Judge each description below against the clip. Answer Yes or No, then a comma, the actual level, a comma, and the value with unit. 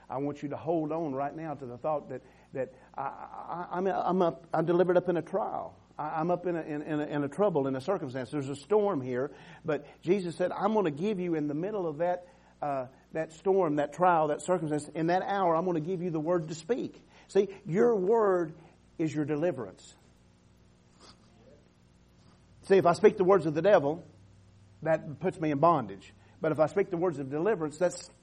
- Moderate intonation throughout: Yes, average, 4.1 semitones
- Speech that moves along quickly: Yes, fast, 220 wpm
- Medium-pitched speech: Yes, medium, 160 Hz